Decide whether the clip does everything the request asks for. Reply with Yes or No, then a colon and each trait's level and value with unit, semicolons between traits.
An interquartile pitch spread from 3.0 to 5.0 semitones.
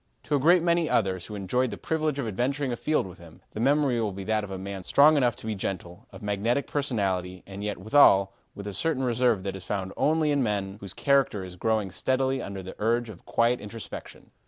No: wide, 5.6 semitones